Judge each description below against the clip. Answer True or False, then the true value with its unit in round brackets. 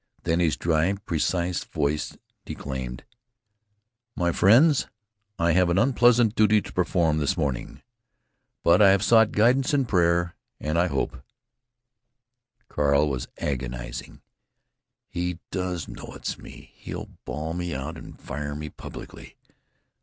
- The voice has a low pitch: True (85 Hz)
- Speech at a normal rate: False (130 wpm)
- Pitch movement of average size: True (4.7 semitones)